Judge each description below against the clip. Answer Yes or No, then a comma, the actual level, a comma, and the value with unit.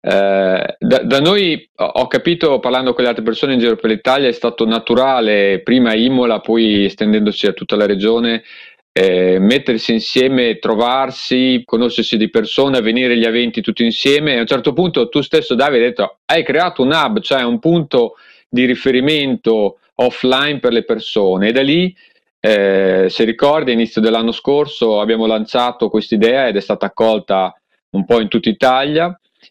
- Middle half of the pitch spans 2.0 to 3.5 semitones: Yes, average, 3.0 semitones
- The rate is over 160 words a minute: Yes, fast, 170 wpm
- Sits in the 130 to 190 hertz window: No, low, 115 Hz